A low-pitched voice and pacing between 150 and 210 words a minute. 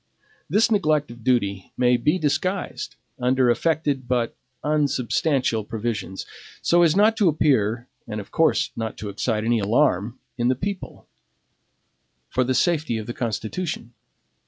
No: low, 125 Hz; average, 140 wpm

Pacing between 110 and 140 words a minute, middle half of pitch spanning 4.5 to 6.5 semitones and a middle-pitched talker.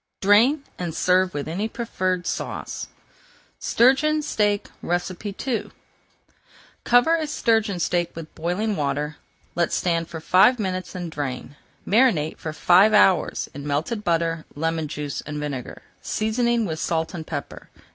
Yes: slow, 135 wpm; average, 5.3 semitones; medium, 180 Hz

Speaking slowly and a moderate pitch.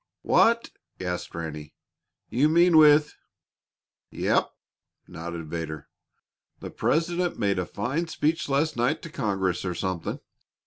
No: slow, 125 wpm; low, 120 Hz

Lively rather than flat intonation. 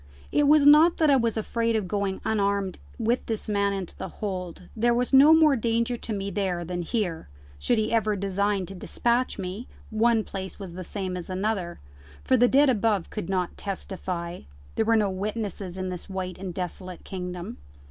No: average, 3.8 semitones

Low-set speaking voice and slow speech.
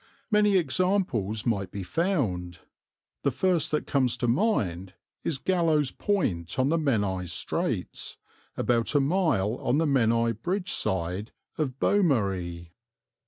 Yes: low, 125 Hz; slow, 125 wpm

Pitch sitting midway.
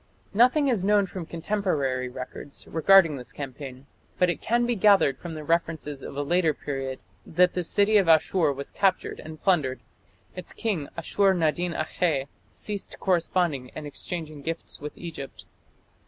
Yes: medium, 165 Hz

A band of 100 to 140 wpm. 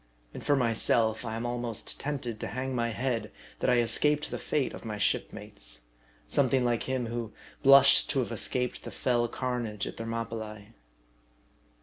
No: average, 160 wpm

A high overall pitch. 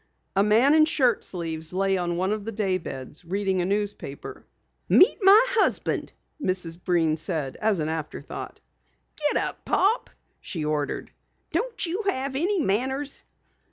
Yes: high, 195 Hz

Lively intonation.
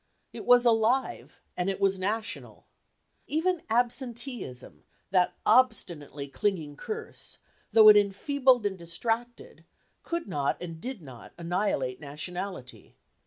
Yes: wide, 6.4 semitones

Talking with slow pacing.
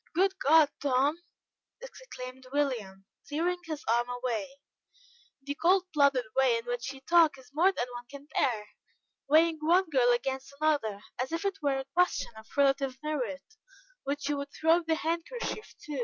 No: average, 165 wpm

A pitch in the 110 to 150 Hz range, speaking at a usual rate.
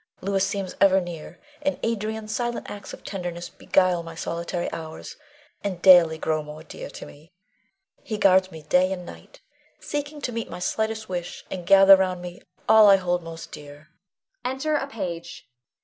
No: medium, 185 Hz; average, 170 wpm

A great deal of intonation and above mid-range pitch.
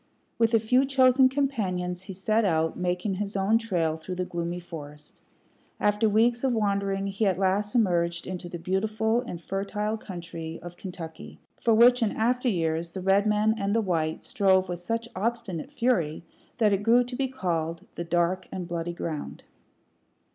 No: average, 4.4 semitones; high, 195 Hz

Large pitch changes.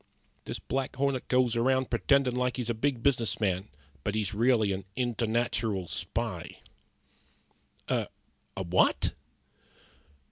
No: average, 3.2 semitones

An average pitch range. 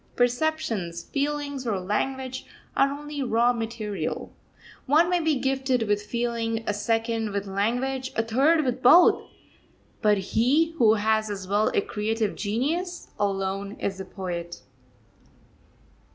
Yes: average, 4.6 semitones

